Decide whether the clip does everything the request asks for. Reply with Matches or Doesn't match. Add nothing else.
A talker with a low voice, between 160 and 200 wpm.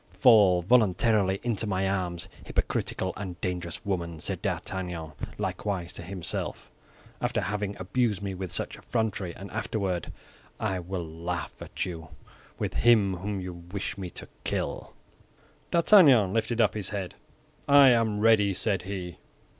Doesn't match